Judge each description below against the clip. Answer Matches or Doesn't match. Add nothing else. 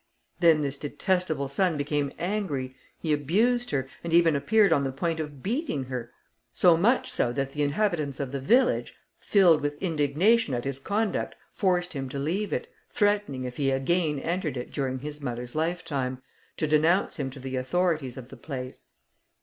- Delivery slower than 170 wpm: Doesn't match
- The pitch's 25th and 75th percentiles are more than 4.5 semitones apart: Matches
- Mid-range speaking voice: Matches